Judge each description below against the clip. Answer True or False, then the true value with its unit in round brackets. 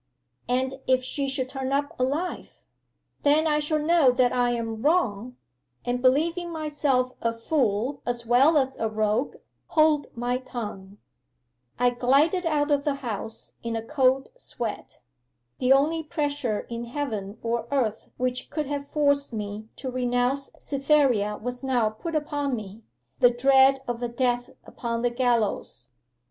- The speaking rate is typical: True (150 wpm)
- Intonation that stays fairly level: False (3.4 semitones)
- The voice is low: False (255 Hz)